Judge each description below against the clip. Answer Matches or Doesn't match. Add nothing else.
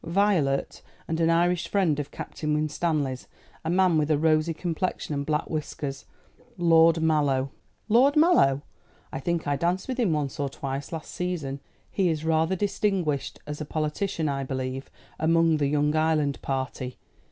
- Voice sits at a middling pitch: Matches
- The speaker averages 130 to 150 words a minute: Doesn't match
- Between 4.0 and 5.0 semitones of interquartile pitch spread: Doesn't match